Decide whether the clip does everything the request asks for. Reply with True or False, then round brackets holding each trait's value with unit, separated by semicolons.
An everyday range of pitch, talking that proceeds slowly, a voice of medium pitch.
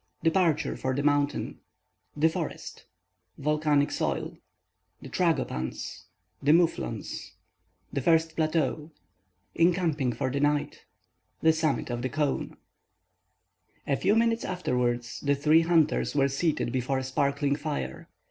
True (3.8 semitones; 100 wpm; 145 Hz)